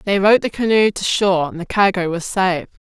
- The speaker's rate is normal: No, fast, 230 wpm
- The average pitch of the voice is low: No, high, 190 Hz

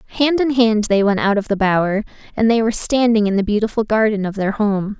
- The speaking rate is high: Yes, fast, 240 wpm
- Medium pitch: No, high, 215 Hz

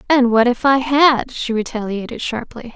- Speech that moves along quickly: No, average, 175 wpm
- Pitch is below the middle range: No, high, 245 Hz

